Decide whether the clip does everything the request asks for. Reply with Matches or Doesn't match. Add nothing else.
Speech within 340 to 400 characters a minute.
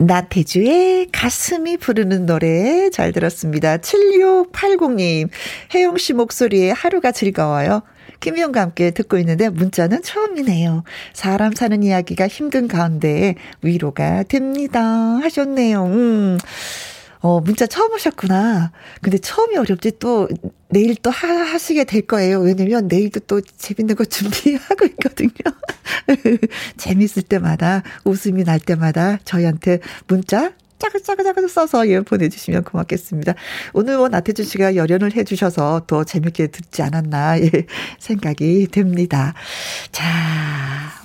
Doesn't match